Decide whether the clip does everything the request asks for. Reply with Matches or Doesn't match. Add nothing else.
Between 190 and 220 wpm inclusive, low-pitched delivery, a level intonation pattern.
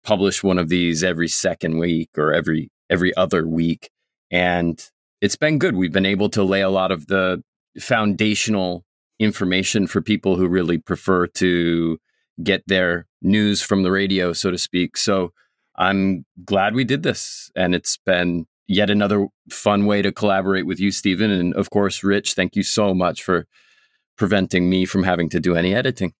Doesn't match